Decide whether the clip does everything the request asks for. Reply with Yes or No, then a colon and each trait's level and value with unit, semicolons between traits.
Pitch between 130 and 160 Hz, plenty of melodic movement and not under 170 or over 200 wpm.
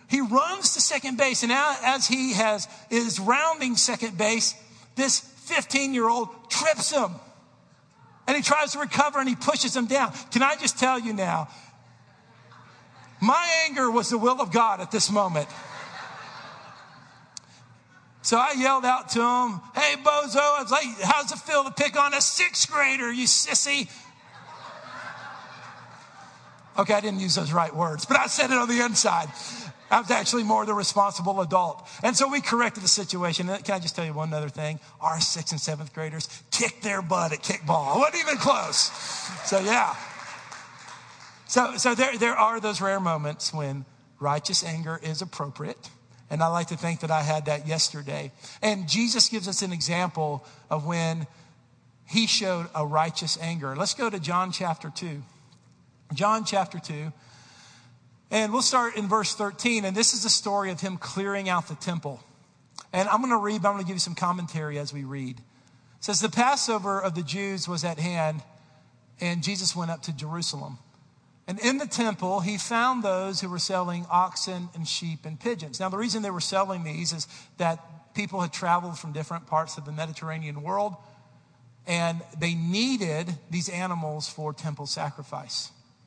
No: high, 190 Hz; wide, 6.8 semitones; average, 175 wpm